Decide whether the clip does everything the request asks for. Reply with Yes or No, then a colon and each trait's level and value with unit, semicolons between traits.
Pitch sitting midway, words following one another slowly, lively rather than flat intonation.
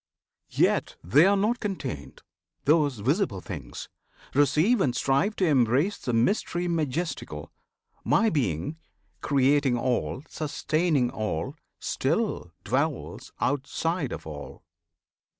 Yes: medium, 145 Hz; slow, 105 wpm; wide, 6.0 semitones